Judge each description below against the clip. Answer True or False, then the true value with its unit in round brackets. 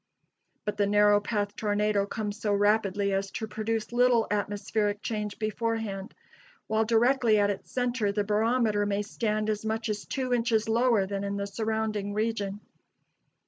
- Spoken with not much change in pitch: True (1.5 semitones)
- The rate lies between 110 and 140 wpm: False (155 wpm)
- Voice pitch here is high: True (210 Hz)